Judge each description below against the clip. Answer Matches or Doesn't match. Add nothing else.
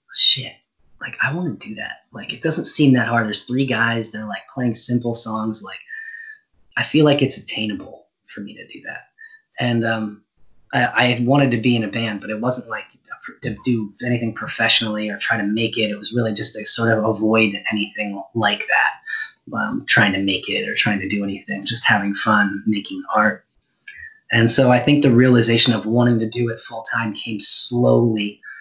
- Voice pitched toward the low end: Matches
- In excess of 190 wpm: Matches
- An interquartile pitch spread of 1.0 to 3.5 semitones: Matches